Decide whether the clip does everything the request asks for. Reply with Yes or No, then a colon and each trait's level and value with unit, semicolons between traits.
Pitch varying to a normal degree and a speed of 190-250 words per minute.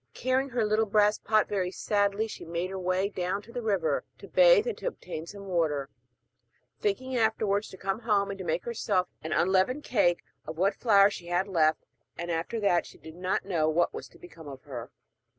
Yes: average, 3.8 semitones; fast, 205 wpm